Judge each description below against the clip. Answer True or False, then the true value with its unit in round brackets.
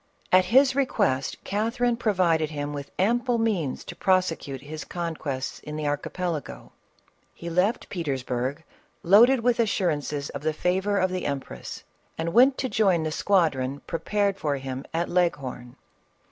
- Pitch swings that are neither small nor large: False (5.8 semitones)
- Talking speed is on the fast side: False (145 wpm)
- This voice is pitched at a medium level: True (170 Hz)